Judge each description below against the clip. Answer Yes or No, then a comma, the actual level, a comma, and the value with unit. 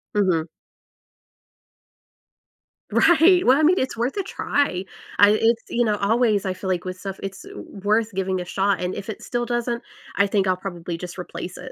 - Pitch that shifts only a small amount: No, average, 4.4 semitones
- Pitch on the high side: Yes, high, 200 Hz